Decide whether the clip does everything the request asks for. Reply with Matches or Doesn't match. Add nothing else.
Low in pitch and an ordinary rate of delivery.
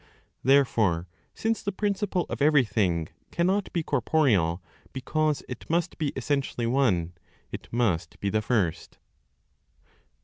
Doesn't match